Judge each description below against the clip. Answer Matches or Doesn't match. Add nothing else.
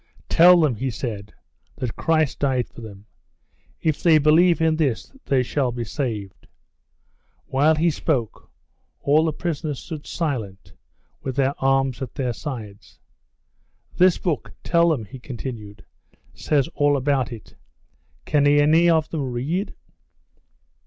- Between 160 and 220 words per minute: Doesn't match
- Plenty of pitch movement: Doesn't match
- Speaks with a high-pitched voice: Doesn't match